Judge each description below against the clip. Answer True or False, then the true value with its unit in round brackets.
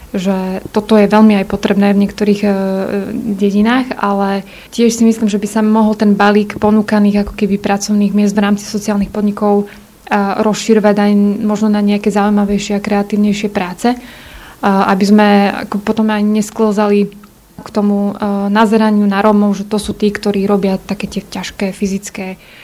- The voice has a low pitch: False (205 Hz)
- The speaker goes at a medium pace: True (150 wpm)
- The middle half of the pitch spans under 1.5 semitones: True (1.0 semitones)